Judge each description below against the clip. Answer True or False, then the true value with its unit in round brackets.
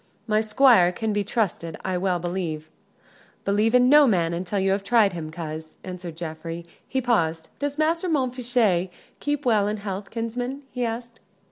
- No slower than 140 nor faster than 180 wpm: True (165 wpm)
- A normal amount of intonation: False (5.9 semitones)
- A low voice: False (205 Hz)